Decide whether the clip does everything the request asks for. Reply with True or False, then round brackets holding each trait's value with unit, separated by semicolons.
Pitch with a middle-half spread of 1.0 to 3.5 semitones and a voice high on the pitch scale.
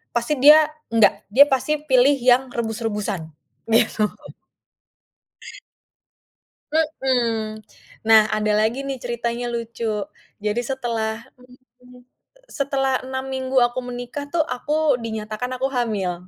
True (3.1 semitones; 240 Hz)